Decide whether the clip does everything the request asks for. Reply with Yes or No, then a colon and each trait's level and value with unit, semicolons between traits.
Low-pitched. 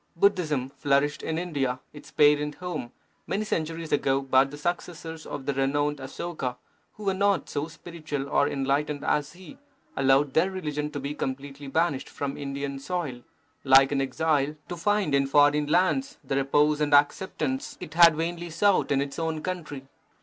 No: medium, 150 Hz